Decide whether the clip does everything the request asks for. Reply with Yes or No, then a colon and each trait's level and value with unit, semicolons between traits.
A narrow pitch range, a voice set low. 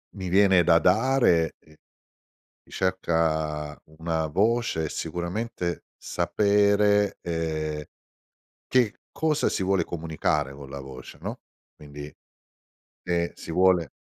No: average, 4.5 semitones; very low, 85 Hz